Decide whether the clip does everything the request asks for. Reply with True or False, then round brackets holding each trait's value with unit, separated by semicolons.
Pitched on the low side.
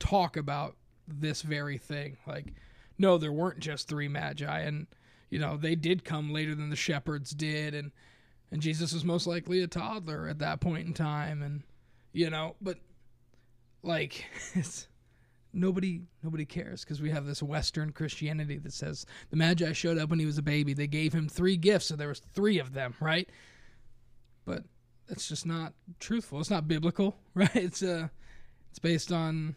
False (155 Hz)